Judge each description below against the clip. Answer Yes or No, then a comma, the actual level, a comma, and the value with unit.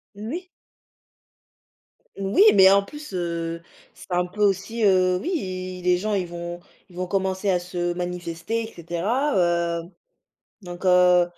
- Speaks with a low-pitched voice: No, medium, 180 Hz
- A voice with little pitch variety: Yes, narrow, 2.3 semitones